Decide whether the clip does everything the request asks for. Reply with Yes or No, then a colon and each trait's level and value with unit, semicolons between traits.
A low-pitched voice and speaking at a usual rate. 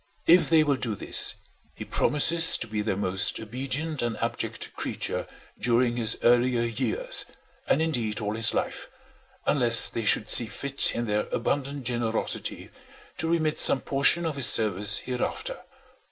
Yes: low, 120 Hz; average, 155 wpm